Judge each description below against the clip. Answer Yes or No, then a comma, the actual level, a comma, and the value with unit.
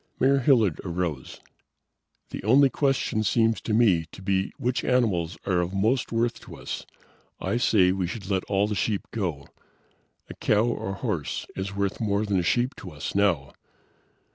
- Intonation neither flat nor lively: Yes, average, 4.1 semitones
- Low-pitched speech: Yes, low, 100 Hz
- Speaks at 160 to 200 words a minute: Yes, average, 175 wpm